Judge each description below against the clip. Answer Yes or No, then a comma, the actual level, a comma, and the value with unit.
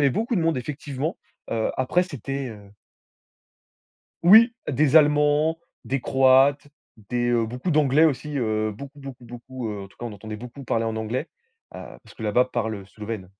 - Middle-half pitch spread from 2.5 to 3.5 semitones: No, average, 4.6 semitones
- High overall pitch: No, low, 130 Hz